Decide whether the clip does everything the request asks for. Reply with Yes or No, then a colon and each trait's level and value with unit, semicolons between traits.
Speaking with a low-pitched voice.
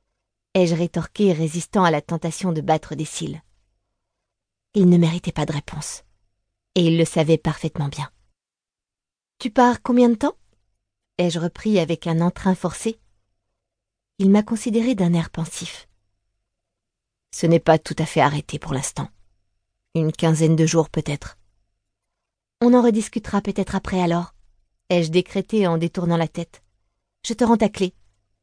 No: medium, 160 Hz